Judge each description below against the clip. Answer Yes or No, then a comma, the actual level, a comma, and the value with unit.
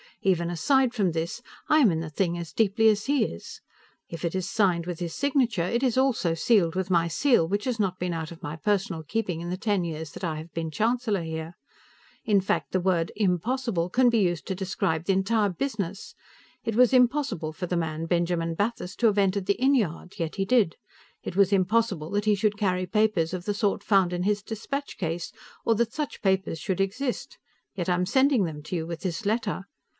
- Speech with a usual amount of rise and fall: Yes, average, 4.6 semitones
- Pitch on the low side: No, high, 190 Hz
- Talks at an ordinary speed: No, fast, 215 wpm